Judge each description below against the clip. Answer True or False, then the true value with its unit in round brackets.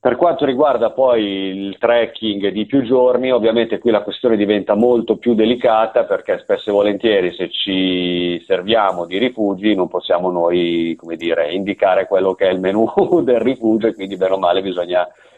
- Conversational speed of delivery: False (175 wpm)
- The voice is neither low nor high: False (105 Hz)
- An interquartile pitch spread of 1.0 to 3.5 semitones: False (4.5 semitones)